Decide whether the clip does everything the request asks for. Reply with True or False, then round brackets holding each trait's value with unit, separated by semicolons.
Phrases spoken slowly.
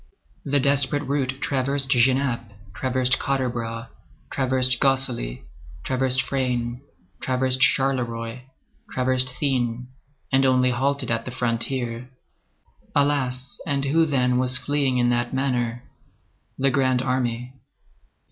True (110 wpm)